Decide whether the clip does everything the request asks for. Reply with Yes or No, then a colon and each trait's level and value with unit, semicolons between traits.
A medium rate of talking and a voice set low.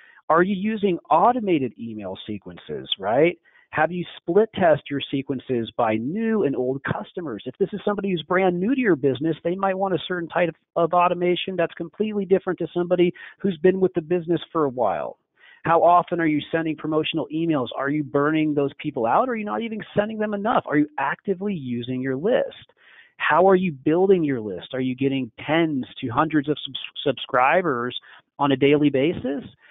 No: average, 195 wpm; medium, 165 Hz